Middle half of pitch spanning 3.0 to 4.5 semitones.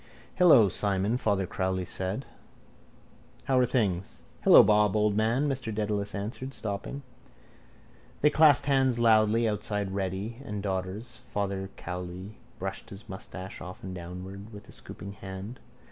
Yes: average, 3.3 semitones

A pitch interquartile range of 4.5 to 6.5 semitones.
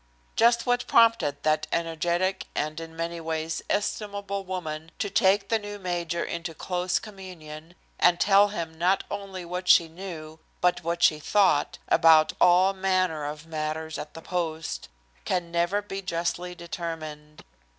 No: average, 3.0 semitones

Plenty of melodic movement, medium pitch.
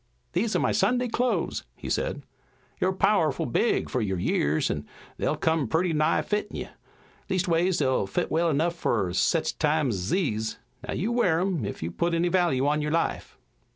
Yes: wide, 6.0 semitones; medium, 165 Hz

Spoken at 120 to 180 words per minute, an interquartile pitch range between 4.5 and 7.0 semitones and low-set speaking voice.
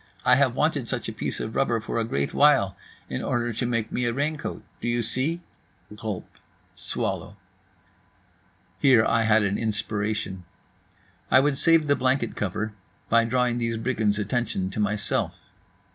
No: average, 160 wpm; average, 3.3 semitones; low, 115 Hz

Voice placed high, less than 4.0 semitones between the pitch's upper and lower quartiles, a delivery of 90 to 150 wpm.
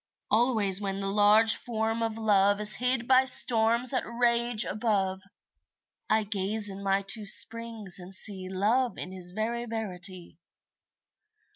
Yes: high, 215 Hz; average, 3.0 semitones; average, 140 wpm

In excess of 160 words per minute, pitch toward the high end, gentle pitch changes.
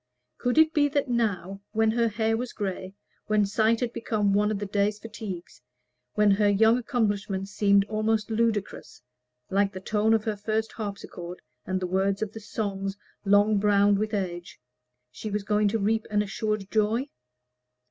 Yes: average, 170 wpm; high, 210 Hz; narrow, 1.9 semitones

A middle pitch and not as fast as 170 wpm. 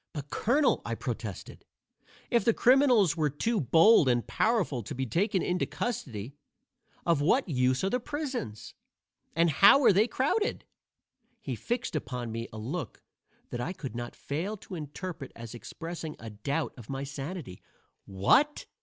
Yes: medium, 160 Hz; average, 155 wpm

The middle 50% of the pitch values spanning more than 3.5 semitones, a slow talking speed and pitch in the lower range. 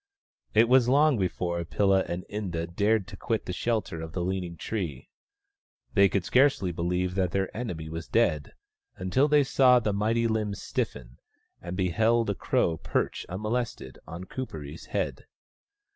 No: average, 4.9 semitones; average, 155 wpm; very low, 95 Hz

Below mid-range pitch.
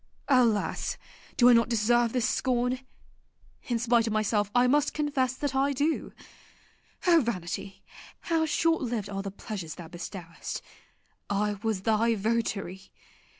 No: high, 230 Hz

